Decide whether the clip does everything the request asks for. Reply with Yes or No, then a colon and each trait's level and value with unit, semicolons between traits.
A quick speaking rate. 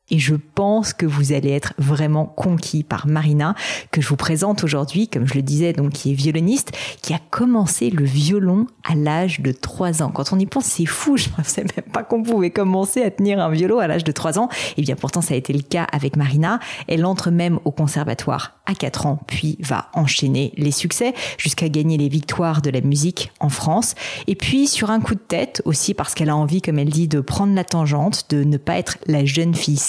Yes: fast, 230 wpm